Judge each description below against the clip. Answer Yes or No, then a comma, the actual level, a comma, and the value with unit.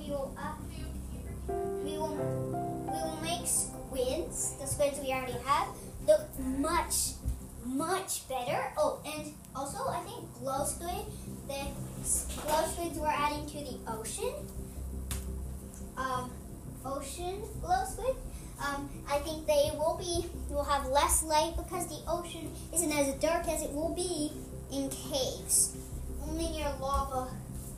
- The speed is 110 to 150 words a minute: Yes, slow, 135 wpm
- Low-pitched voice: No, very high, 265 Hz